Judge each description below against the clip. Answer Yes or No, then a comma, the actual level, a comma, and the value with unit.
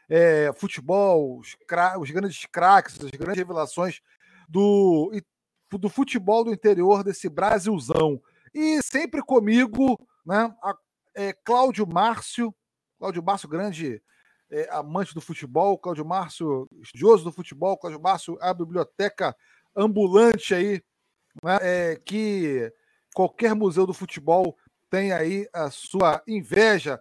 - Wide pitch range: No, average, 4.0 semitones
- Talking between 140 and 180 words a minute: No, slow, 120 wpm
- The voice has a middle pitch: No, high, 195 Hz